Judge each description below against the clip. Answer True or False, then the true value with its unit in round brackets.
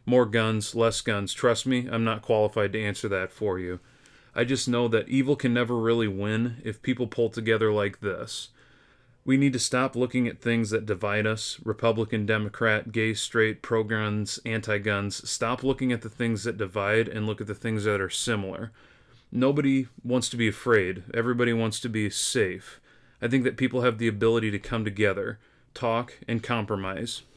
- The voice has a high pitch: False (115 Hz)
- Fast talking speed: False (185 wpm)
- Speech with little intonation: True (2.2 semitones)